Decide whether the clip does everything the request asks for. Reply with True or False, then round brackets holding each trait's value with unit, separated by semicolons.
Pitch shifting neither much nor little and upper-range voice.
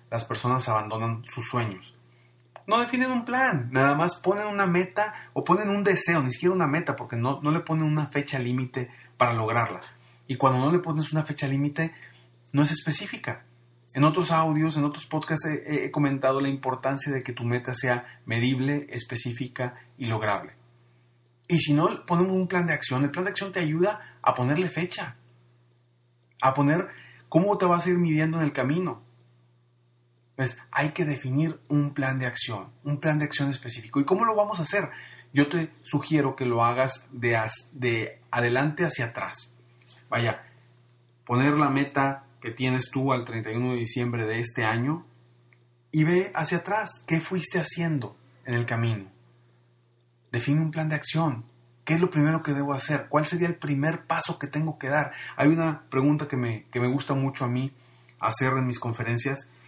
False (4.5 semitones; 135 Hz)